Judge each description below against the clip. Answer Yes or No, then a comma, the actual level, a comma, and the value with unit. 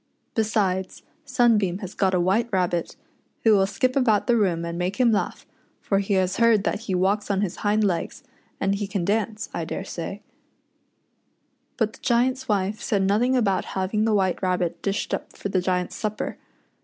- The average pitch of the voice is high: Yes, high, 200 Hz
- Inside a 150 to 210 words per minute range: Yes, average, 180 wpm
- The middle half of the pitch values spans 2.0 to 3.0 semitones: Yes, average, 2.7 semitones